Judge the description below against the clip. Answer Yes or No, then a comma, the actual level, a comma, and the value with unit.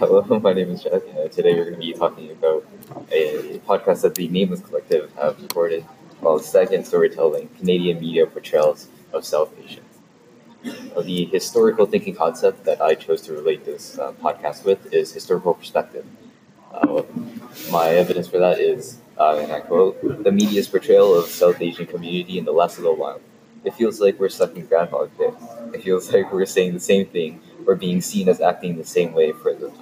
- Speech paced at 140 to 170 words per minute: No, average, 195 wpm